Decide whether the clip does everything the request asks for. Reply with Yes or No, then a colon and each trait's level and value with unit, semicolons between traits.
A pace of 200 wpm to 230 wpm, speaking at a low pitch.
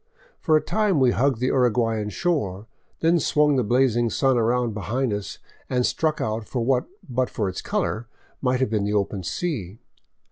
No: average, 180 wpm; low, 125 Hz